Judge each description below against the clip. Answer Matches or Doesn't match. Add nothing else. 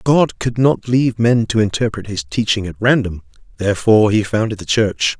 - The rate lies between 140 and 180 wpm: Matches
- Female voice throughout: Doesn't match